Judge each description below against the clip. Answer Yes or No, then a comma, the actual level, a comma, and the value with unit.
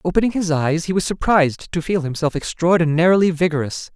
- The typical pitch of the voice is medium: Yes, medium, 165 Hz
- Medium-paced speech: Yes, average, 165 wpm